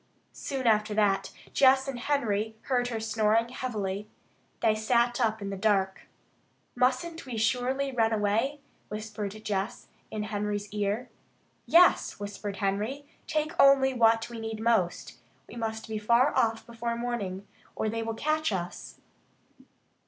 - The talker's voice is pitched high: Yes, high, 225 Hz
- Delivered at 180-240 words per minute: No, average, 140 wpm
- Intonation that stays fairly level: No, average, 3.1 semitones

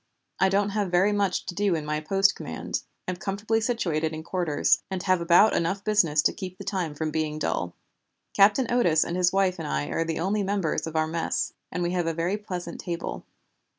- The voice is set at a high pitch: No, medium, 180 Hz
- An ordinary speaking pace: No, fast, 215 wpm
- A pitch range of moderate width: Yes, average, 3.6 semitones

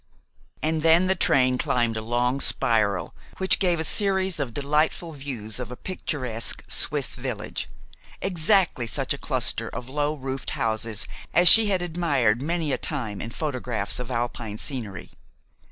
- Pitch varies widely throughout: Yes, wide, 5.9 semitones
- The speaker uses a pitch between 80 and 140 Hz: Yes, low, 135 Hz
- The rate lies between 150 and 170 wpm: Yes, average, 155 wpm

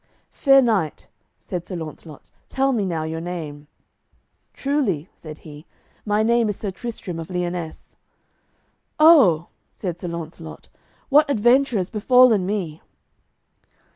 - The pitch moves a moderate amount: No, wide, 6.4 semitones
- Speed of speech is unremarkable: No, slow, 125 wpm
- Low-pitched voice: No, medium, 185 Hz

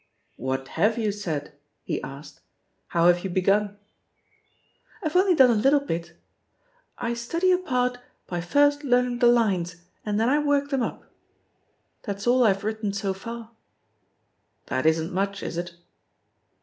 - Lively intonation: Yes, wide, 5.7 semitones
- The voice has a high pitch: Yes, high, 215 Hz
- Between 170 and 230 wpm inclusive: No, average, 150 wpm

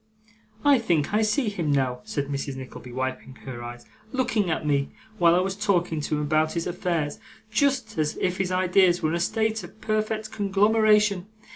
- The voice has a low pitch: No, medium, 180 Hz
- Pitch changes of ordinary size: No, wide, 6.3 semitones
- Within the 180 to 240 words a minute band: Yes, average, 185 wpm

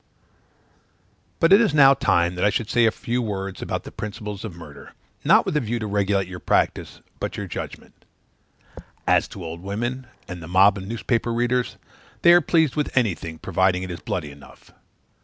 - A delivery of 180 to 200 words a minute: Yes, average, 190 wpm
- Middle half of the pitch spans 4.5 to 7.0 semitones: Yes, average, 4.8 semitones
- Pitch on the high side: No, low, 105 Hz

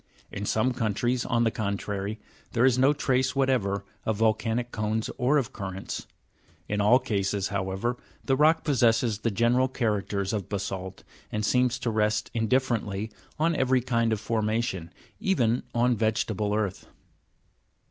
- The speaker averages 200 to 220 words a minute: No, average, 145 wpm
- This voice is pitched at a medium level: No, low, 115 Hz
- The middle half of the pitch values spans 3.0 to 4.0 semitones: Yes, average, 3.5 semitones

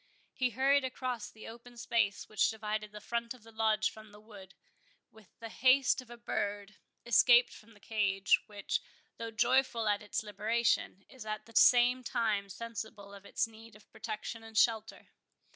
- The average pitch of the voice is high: Yes, high, 220 Hz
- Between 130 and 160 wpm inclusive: No, average, 175 wpm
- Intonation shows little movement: Yes, narrow, 2.1 semitones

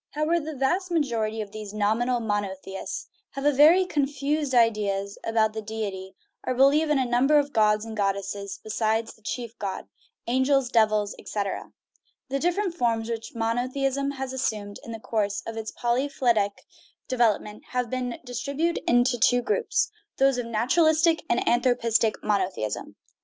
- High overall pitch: Yes, high, 235 Hz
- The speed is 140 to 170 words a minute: Yes, average, 150 wpm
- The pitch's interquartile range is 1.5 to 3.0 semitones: No, average, 4.2 semitones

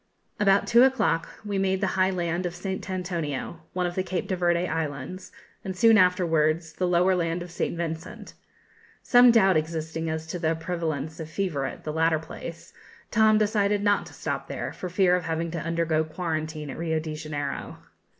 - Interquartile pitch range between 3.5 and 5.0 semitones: No, average, 2.7 semitones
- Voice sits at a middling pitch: Yes, medium, 170 Hz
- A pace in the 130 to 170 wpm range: No, average, 190 wpm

